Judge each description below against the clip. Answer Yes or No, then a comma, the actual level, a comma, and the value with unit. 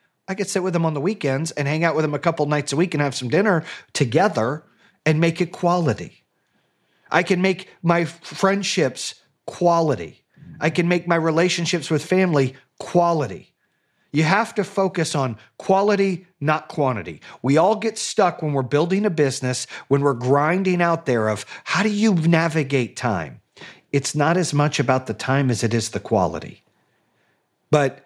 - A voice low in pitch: No, medium, 160 Hz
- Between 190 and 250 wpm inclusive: No, average, 175 wpm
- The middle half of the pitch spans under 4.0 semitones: No, average, 4.5 semitones